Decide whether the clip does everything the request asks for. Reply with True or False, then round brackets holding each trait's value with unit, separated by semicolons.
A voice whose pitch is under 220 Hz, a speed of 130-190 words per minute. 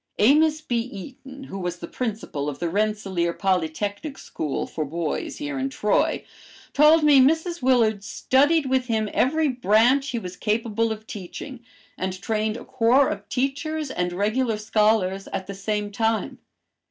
False (225 Hz; 155 wpm)